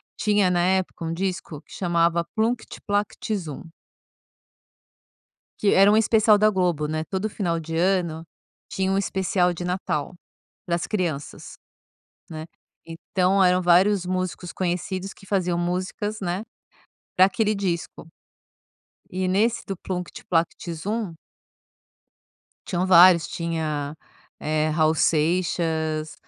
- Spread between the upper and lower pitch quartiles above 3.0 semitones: No, average, 2.7 semitones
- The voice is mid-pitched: Yes, medium, 180 Hz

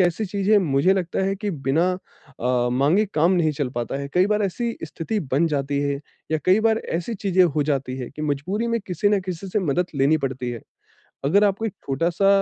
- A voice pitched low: No, medium, 170 Hz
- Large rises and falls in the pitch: Yes, wide, 6.0 semitones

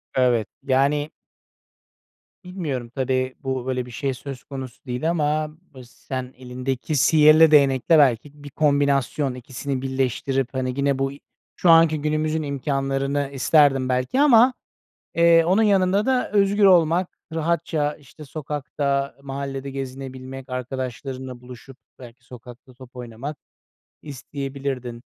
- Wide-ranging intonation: No, average, 3.0 semitones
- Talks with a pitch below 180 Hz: Yes, low, 135 Hz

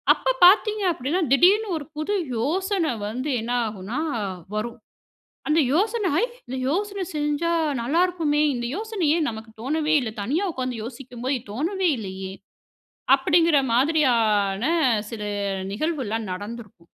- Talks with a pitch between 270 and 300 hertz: Yes, very high, 280 Hz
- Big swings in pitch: Yes, wide, 6.7 semitones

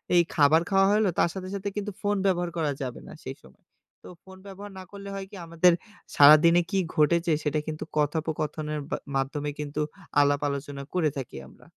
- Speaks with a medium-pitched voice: Yes, medium, 160 Hz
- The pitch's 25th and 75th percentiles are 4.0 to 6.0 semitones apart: Yes, average, 4.3 semitones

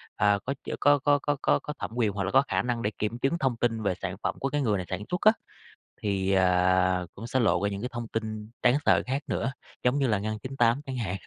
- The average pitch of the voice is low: Yes, low, 115 Hz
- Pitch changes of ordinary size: Yes, average, 4.9 semitones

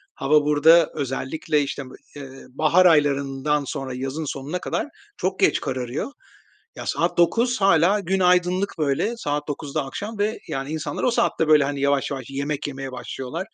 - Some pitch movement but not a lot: Yes, average, 4.5 semitones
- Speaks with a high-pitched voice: No, medium, 150 Hz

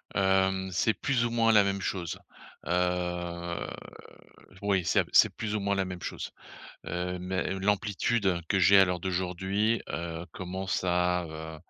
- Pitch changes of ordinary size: No, narrow, 2.0 semitones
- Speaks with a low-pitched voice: Yes, very low, 95 Hz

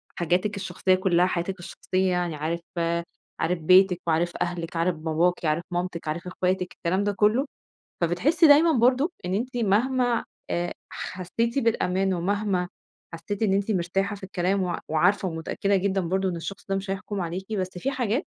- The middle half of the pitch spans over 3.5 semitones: No, average, 2.7 semitones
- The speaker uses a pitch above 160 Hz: Yes, medium, 185 Hz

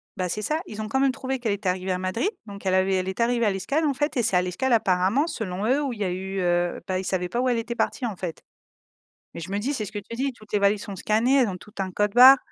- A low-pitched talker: No, high, 210 Hz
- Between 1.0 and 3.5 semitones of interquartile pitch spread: No, average, 4.9 semitones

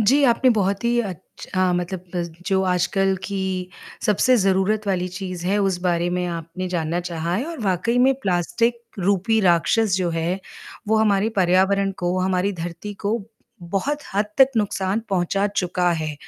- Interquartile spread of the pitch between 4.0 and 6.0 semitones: No, average, 2.8 semitones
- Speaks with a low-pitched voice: No, high, 190 Hz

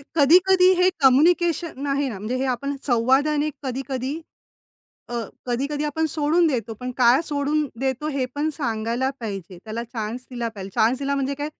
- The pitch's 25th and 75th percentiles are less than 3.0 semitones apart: No, average, 3.8 semitones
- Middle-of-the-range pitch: No, very high, 270 Hz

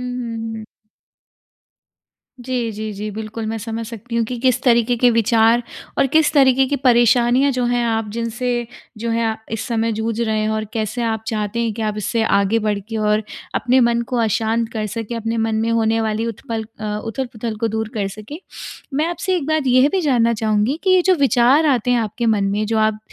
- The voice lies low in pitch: No, high, 230 Hz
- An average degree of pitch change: No, narrow, 2.1 semitones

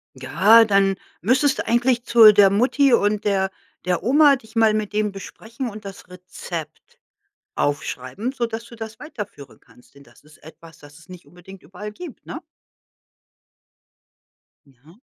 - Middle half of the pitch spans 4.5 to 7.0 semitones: Yes, average, 4.8 semitones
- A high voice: Yes, high, 205 Hz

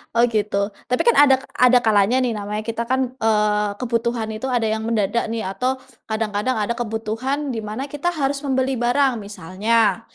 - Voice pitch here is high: Yes, high, 230 Hz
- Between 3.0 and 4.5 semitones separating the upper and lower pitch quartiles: Yes, average, 3.3 semitones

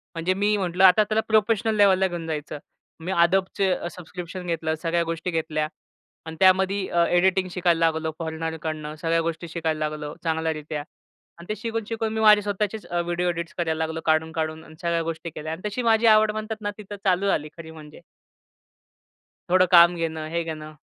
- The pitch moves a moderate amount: Yes, average, 3.2 semitones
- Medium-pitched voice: Yes, medium, 170 Hz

